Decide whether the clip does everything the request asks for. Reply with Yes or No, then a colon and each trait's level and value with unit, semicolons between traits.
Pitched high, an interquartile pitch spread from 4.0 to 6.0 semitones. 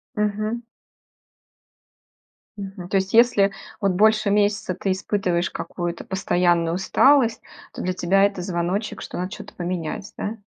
No: high, 195 Hz; narrow, 2.6 semitones